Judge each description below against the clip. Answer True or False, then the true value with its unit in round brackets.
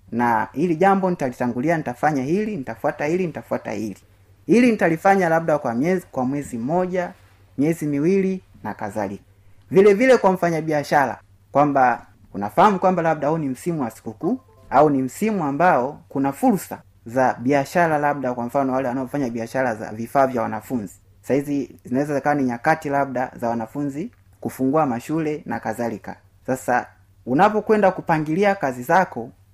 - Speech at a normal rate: False (150 wpm)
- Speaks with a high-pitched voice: False (140 Hz)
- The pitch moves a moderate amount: False (6.3 semitones)